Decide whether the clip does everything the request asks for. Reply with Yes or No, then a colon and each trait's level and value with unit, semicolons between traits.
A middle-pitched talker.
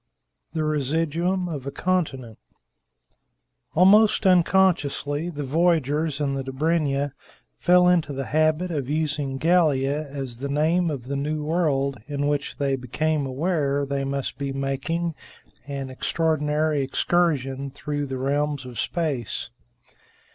Yes: medium, 145 Hz